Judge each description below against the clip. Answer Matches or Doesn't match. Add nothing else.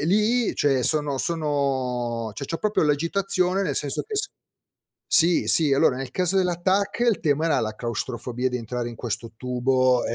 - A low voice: Doesn't match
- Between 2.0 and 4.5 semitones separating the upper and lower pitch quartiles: Doesn't match